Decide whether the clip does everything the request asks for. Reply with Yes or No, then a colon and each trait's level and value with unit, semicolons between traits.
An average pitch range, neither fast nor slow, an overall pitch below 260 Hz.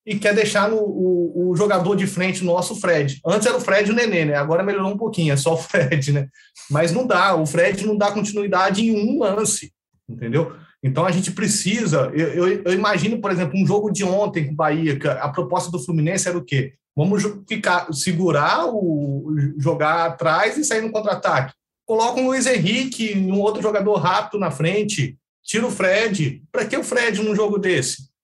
No: average, 4.4 semitones; fast, 205 wpm; medium, 185 Hz